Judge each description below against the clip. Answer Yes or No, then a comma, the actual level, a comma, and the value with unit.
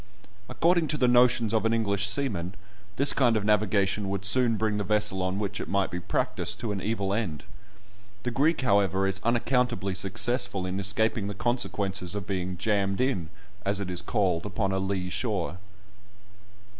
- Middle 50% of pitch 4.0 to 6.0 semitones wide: No, average, 3.2 semitones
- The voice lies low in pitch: Yes, low, 100 Hz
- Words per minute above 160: Yes, average, 175 wpm